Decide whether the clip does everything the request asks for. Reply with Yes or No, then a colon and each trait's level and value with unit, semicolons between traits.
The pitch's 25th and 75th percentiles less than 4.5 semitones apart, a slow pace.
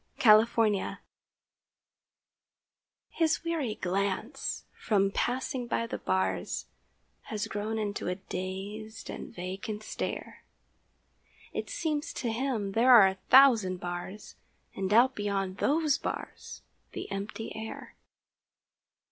Yes: average, 4.0 semitones; slow, 110 wpm